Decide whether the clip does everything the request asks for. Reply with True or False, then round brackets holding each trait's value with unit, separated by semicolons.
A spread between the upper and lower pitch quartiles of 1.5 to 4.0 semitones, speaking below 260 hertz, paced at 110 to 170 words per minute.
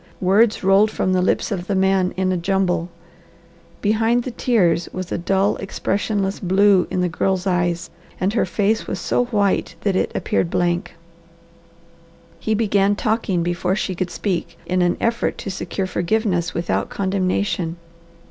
True (2.4 semitones; 190 Hz; 160 wpm)